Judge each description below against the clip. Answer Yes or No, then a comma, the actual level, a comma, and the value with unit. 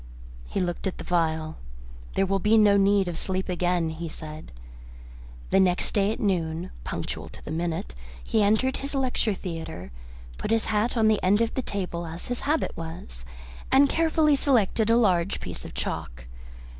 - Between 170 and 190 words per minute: Yes, average, 180 wpm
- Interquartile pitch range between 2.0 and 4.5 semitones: No, average, 4.9 semitones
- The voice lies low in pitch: No, high, 190 Hz